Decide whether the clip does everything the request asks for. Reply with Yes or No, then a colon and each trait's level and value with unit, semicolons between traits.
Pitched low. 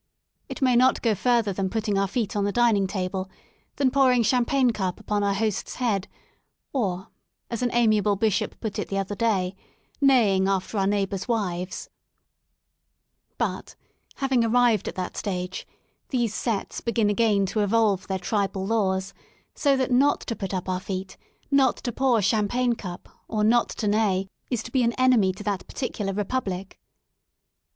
No: high, 210 Hz